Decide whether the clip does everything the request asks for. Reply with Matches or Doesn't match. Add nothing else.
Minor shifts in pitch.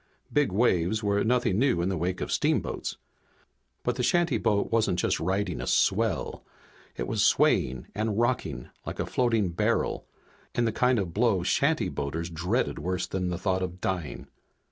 Doesn't match